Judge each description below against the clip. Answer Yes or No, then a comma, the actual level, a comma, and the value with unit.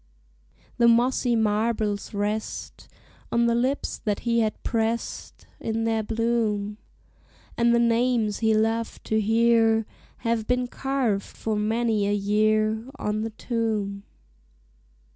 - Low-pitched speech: No, high, 225 Hz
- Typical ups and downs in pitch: No, narrow, 1.6 semitones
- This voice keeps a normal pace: No, slow, 125 wpm